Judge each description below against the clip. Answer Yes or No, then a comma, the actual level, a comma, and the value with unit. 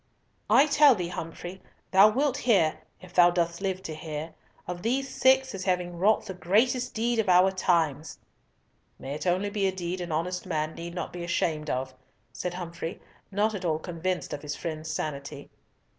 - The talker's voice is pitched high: No, medium, 180 Hz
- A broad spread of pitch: No, average, 3.6 semitones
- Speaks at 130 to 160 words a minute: No, average, 175 wpm